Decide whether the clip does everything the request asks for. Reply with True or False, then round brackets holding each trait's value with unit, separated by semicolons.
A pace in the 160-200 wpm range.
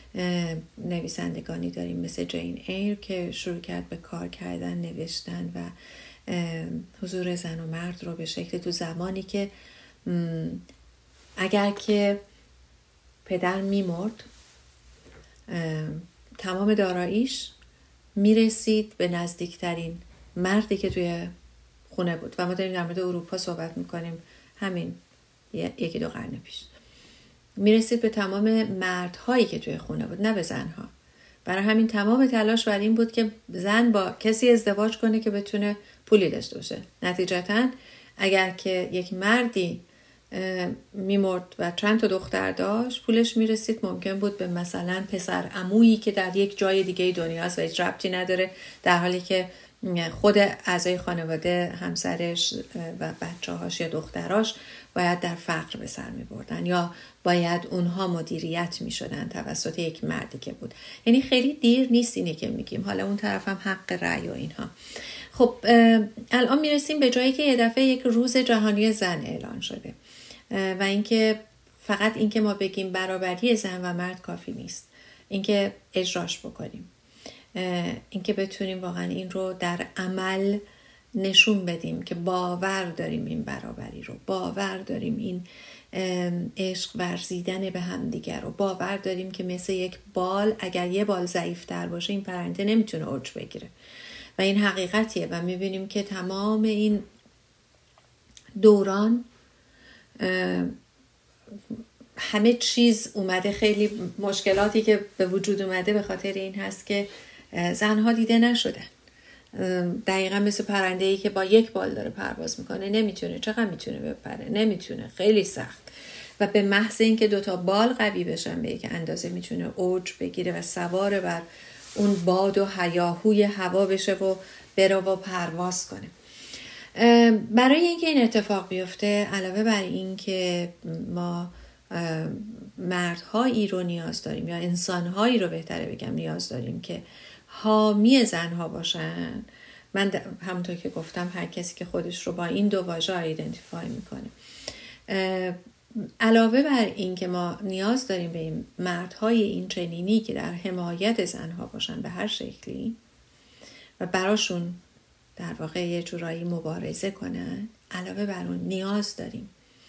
False (140 wpm)